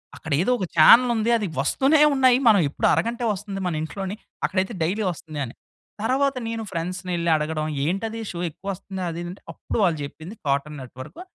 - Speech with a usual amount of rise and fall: No, wide, 5.9 semitones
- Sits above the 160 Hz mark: Yes, medium, 185 Hz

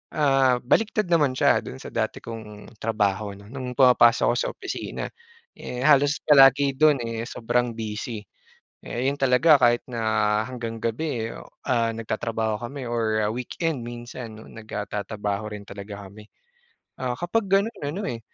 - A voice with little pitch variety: No, average, 3.8 semitones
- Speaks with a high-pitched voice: No, low, 120 Hz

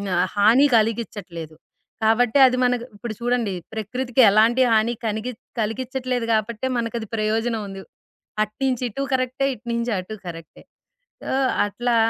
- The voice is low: No, high, 230 Hz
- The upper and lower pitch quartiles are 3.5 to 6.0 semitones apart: No, average, 2.7 semitones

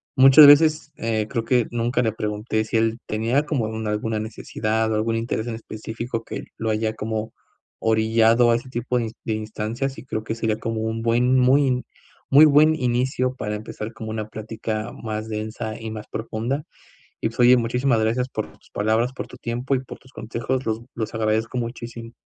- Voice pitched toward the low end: Yes, low, 115 Hz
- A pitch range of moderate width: No, narrow, 2.2 semitones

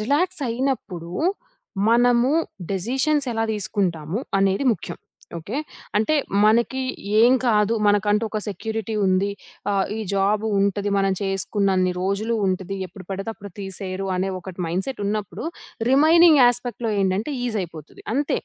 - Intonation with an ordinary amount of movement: Yes, average, 3.7 semitones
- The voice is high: Yes, high, 205 Hz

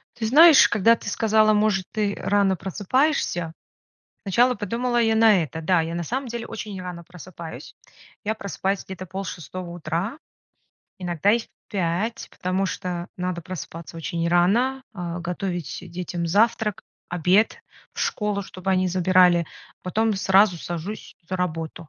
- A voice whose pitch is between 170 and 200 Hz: Yes, high, 190 Hz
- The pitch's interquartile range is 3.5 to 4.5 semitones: Yes, average, 3.8 semitones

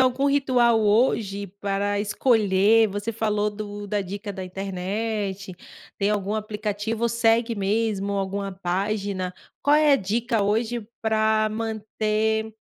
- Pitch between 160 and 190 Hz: No, high, 210 Hz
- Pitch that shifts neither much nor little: No, narrow, 2.1 semitones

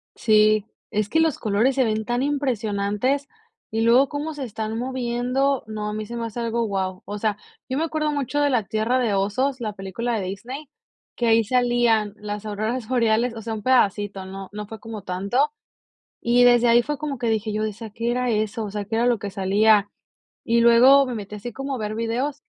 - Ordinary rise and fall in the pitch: Yes, average, 3.1 semitones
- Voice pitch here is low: No, high, 230 Hz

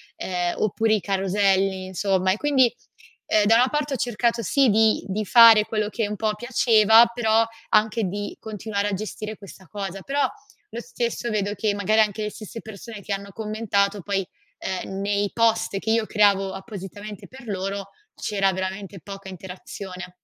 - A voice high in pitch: Yes, high, 210 Hz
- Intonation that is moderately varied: No, narrow, 2.2 semitones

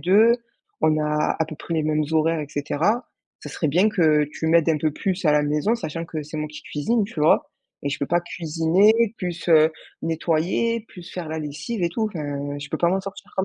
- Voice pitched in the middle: Yes, medium, 160 Hz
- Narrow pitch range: No, average, 3.7 semitones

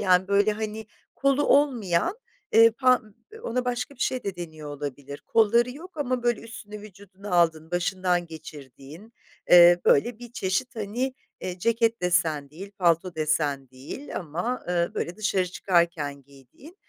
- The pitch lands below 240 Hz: Yes, high, 190 Hz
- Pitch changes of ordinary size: No, wide, 6.1 semitones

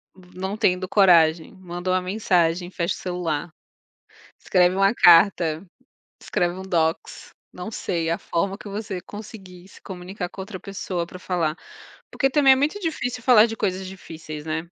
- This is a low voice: No, medium, 185 Hz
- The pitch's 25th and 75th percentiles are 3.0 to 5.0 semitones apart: No, narrow, 2.5 semitones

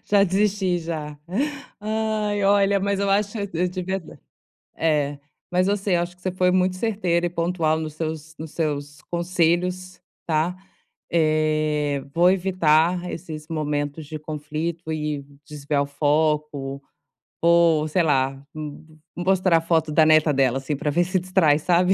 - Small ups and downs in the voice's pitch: No, average, 3.2 semitones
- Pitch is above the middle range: No, medium, 165 Hz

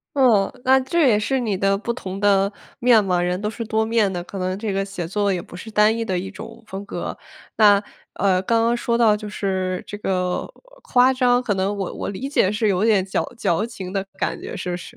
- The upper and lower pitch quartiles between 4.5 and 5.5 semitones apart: No, average, 3.2 semitones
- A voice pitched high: Yes, high, 205 Hz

